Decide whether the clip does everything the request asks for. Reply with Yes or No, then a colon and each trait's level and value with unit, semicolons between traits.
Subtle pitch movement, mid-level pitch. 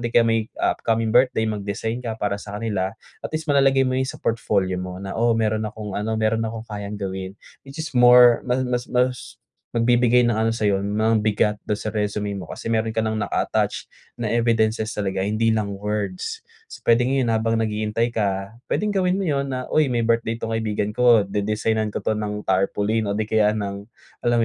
No: narrow, 2.2 semitones; low, 110 Hz